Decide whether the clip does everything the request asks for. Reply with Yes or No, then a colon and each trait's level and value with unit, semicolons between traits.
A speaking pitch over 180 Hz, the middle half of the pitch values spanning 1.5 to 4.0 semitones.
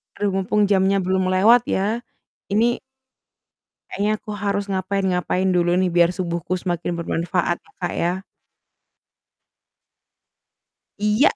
Yes: high, 190 Hz; narrow, 2.4 semitones